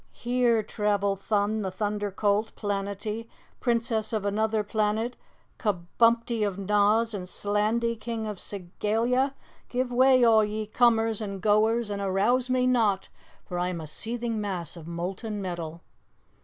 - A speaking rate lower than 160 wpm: Yes, average, 140 wpm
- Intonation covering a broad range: No, narrow, 2.5 semitones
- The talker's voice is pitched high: Yes, high, 210 Hz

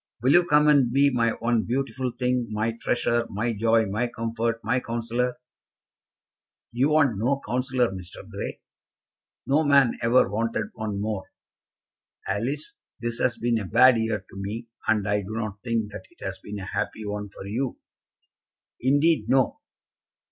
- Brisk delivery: No, average, 160 wpm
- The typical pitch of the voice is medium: No, low, 115 Hz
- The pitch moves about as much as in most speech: Yes, average, 3.0 semitones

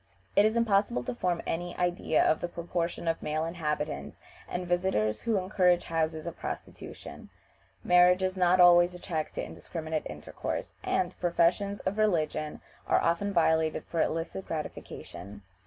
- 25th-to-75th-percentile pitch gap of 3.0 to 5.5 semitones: No, narrow, 2.4 semitones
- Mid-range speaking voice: Yes, medium, 175 Hz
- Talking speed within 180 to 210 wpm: No, average, 150 wpm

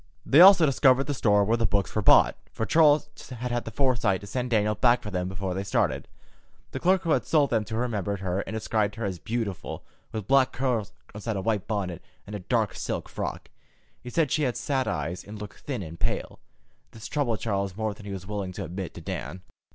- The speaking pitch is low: Yes, low, 110 Hz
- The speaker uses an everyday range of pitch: Yes, average, 4.1 semitones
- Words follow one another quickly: Yes, fast, 230 wpm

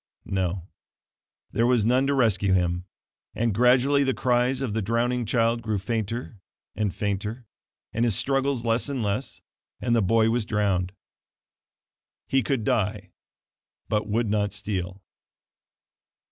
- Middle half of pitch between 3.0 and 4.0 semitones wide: Yes, average, 3.3 semitones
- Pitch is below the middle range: Yes, low, 115 Hz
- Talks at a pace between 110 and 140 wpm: Yes, slow, 135 wpm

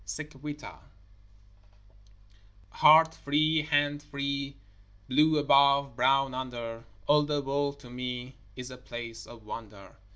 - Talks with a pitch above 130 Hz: Yes, medium, 140 Hz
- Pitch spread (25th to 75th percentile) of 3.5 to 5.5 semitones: No, average, 2.9 semitones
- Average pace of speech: No, slow, 120 wpm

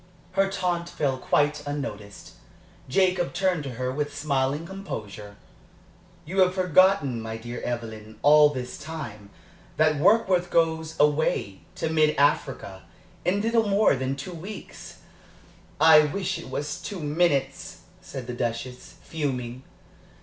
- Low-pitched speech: No, medium, 150 Hz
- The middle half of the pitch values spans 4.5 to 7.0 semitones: Yes, wide, 5.6 semitones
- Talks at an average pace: No, slow, 130 wpm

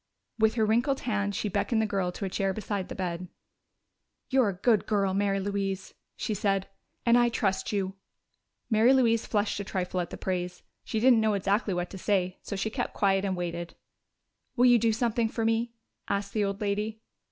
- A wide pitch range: No, average, 2.7 semitones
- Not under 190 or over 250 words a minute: Yes, average, 200 wpm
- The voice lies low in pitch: No, high, 205 Hz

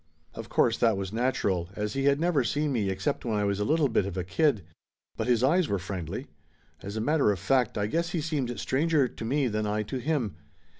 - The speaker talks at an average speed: No, fast, 235 wpm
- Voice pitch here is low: Yes, low, 115 Hz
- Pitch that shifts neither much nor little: No, wide, 6.0 semitones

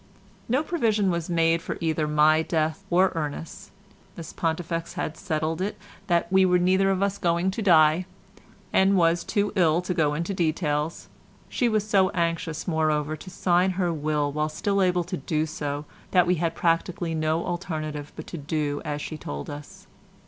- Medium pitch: Yes, medium, 170 Hz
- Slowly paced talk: No, average, 175 wpm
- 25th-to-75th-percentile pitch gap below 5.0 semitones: Yes, average, 3.1 semitones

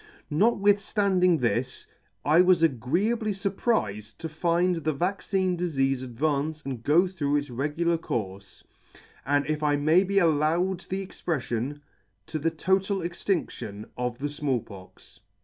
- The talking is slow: Yes, slow, 130 wpm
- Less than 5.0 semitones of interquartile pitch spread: No, average, 5.3 semitones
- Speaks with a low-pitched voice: No, medium, 155 Hz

